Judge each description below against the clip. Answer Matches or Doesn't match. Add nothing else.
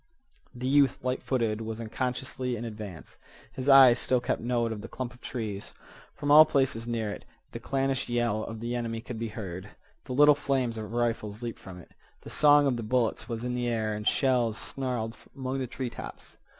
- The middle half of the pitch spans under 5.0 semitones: Matches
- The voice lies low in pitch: Matches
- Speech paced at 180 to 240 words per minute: Matches